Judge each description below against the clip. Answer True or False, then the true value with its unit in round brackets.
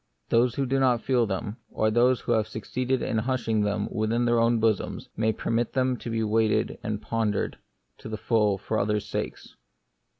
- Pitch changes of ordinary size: False (1.9 semitones)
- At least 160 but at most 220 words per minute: True (190 wpm)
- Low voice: True (115 Hz)